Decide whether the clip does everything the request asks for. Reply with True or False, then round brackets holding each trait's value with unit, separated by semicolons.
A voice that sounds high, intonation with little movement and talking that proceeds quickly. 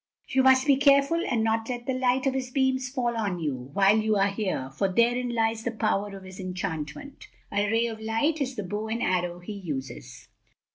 False (225 Hz; 4.8 semitones; 210 wpm)